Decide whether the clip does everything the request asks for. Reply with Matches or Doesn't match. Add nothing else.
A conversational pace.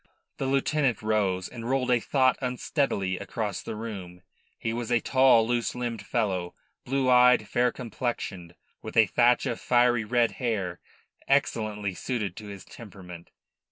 Matches